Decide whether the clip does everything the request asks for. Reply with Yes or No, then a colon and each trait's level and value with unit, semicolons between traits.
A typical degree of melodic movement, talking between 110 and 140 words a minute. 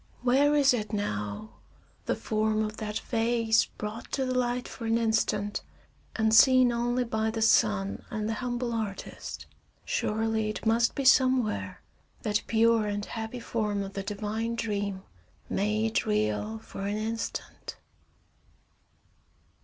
No: narrow, 2.0 semitones; slow, 135 wpm